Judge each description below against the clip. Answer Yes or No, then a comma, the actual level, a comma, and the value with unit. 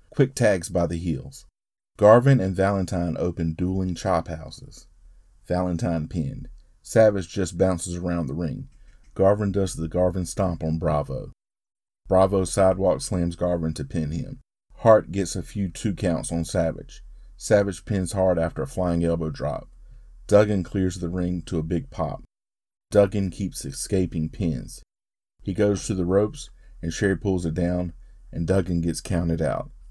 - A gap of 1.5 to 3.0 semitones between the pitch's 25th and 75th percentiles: Yes, narrow, 2.4 semitones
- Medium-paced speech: Yes, average, 155 wpm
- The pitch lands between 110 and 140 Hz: No, very low, 90 Hz